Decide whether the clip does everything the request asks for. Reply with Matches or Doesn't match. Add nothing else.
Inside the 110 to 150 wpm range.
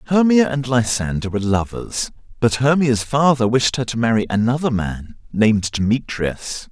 Matches